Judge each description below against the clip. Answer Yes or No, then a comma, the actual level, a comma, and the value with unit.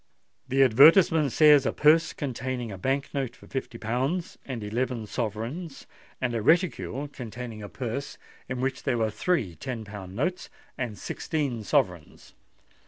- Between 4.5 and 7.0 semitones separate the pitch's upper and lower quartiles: No, average, 4.1 semitones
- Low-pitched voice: Yes, low, 130 Hz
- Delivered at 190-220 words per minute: No, average, 150 wpm